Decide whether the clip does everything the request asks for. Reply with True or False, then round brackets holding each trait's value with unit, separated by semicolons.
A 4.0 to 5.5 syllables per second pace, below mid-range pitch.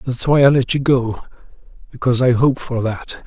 True (5.3 syllables/s; 125 Hz)